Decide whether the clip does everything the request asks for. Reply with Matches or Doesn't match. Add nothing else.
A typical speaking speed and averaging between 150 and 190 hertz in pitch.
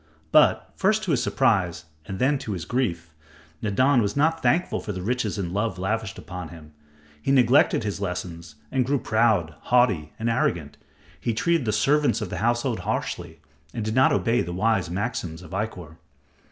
Doesn't match